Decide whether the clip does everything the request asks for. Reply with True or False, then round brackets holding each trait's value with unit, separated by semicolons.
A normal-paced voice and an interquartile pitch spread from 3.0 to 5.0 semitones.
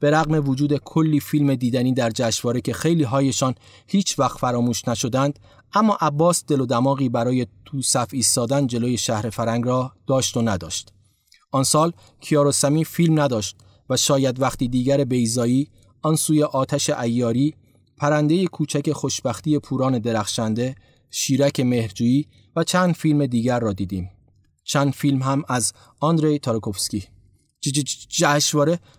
True (135 wpm; 3.9 semitones)